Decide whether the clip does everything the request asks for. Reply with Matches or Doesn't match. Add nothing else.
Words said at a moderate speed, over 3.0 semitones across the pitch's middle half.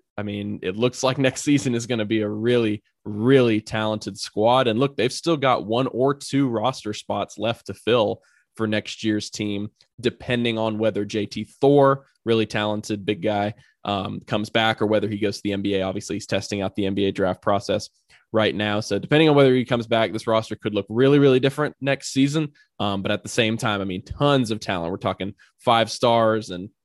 Doesn't match